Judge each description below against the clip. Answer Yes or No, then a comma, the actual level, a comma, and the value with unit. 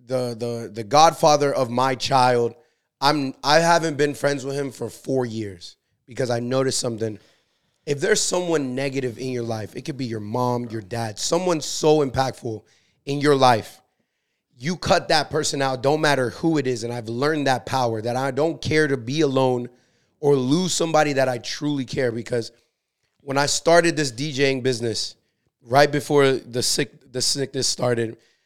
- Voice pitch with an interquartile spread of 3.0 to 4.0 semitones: Yes, average, 3.4 semitones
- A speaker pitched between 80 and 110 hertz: No, low, 135 Hz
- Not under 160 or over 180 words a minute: Yes, average, 175 wpm